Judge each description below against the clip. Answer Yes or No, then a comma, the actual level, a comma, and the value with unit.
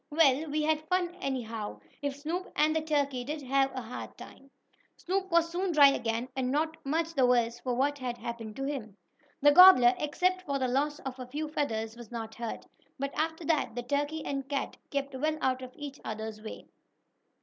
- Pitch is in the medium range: No, very high, 275 Hz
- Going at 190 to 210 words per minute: Yes, average, 200 wpm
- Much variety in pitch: No, average, 3.9 semitones